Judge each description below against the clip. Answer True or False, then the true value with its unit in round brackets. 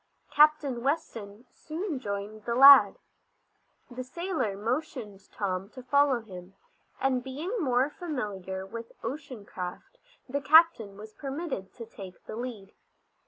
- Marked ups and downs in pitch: True (5.8 semitones)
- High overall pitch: True (245 Hz)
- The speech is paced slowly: True (125 wpm)